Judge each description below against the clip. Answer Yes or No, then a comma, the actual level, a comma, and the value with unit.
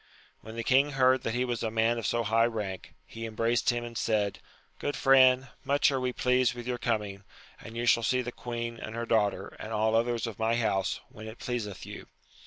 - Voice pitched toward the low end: Yes, low, 115 Hz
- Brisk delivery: Yes, fast, 220 wpm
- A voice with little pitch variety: Yes, narrow, 2.0 semitones